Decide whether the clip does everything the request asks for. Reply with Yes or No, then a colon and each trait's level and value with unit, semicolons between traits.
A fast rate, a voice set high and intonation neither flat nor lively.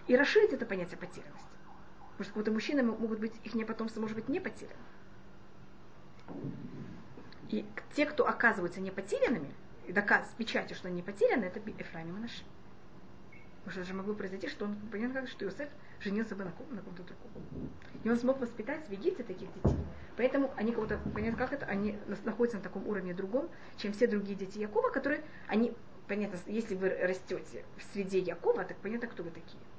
Yes: fast, 185 wpm; high, 220 Hz; average, 3.8 semitones